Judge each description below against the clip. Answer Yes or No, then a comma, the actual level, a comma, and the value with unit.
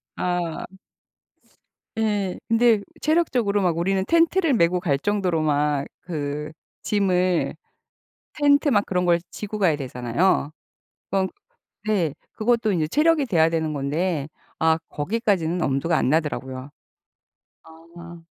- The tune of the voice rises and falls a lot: No, average, 4.9 semitones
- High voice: No, medium, 180 Hz